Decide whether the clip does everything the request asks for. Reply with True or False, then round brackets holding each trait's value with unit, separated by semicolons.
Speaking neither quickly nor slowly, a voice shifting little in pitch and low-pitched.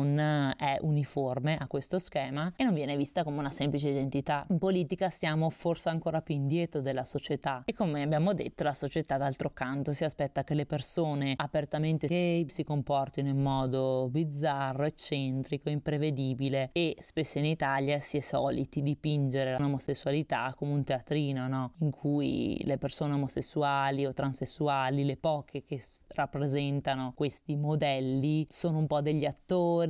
False (150 wpm; 2.0 semitones; 145 Hz)